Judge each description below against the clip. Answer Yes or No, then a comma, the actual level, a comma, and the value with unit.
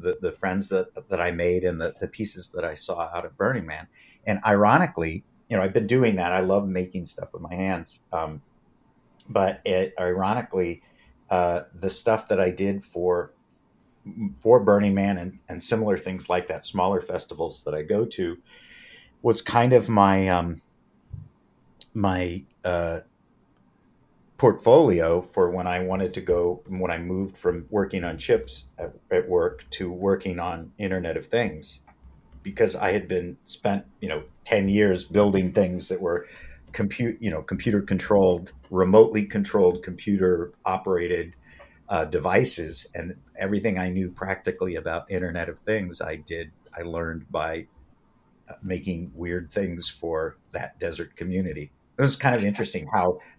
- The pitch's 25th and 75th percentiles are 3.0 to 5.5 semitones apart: No, narrow, 2.5 semitones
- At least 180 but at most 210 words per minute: No, average, 155 wpm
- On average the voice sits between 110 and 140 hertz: No, very low, 90 Hz